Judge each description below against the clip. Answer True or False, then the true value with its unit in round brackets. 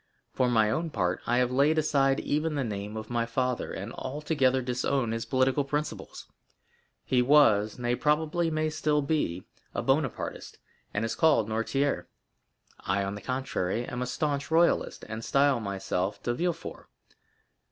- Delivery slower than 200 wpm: True (150 wpm)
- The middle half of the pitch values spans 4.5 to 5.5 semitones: True (5.0 semitones)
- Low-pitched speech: True (125 Hz)